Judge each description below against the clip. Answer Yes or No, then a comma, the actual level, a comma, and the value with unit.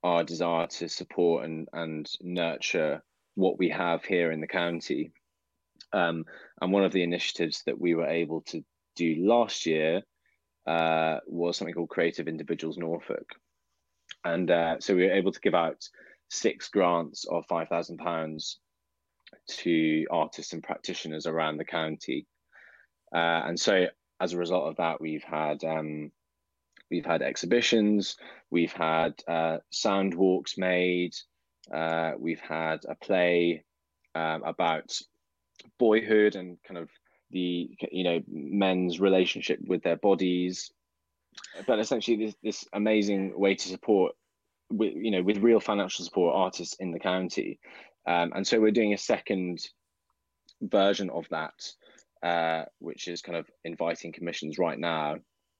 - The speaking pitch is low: Yes, very low, 85 Hz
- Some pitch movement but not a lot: No, narrow, 2.3 semitones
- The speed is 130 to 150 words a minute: Yes, average, 140 wpm